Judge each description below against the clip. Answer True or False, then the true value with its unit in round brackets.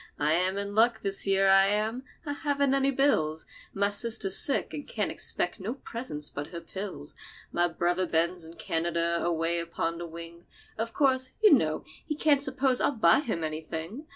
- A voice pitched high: True (195 Hz)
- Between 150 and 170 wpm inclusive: False (180 wpm)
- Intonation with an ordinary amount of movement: False (7.3 semitones)